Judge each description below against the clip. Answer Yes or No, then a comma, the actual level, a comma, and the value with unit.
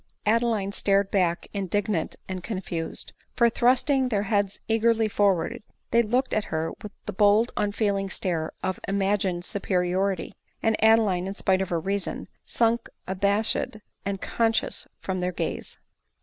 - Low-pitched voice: No, high, 200 Hz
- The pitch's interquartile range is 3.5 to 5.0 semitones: No, average, 2.9 semitones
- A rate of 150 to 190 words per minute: No, average, 140 wpm